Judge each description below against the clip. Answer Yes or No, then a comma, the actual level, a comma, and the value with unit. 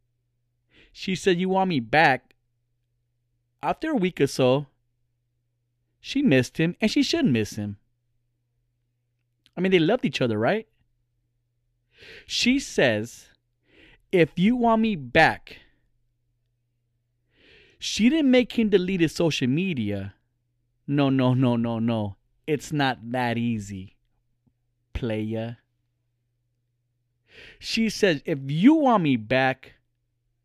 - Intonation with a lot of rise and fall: No, average, 4.8 semitones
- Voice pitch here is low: Yes, low, 120 Hz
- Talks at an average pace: No, slow, 115 wpm